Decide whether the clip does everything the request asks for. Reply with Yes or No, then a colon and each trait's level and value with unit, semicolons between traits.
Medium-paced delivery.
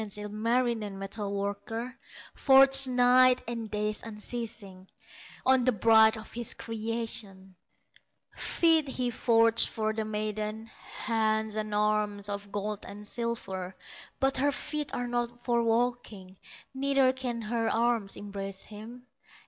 No: slow, 125 wpm